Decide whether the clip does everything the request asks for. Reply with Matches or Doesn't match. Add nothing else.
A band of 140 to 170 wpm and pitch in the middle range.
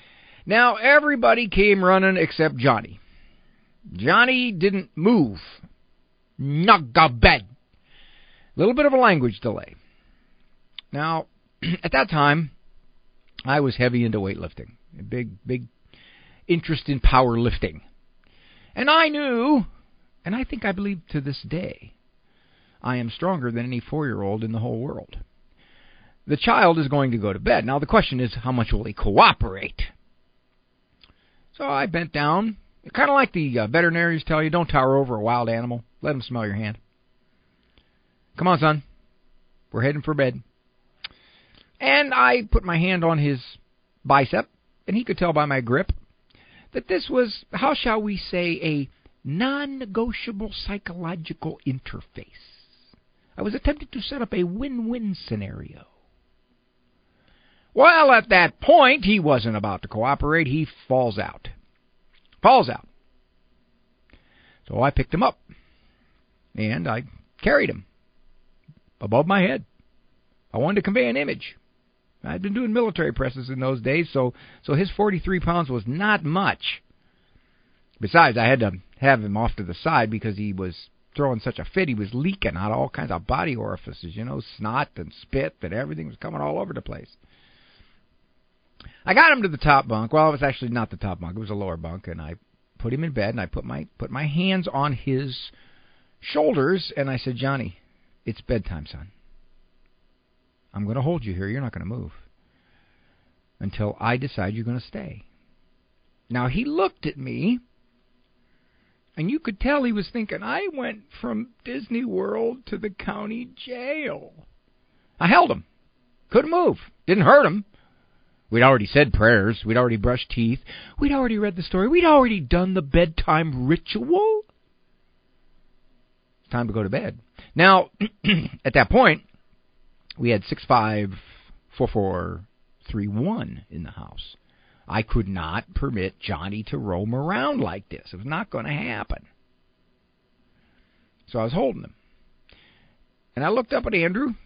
Doesn't match